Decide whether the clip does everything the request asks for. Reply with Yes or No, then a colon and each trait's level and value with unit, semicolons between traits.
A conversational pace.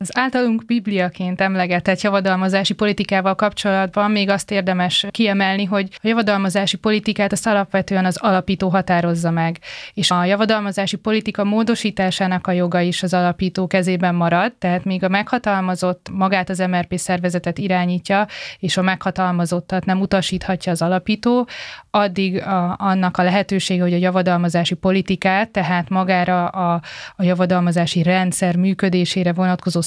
Yes: average, 135 wpm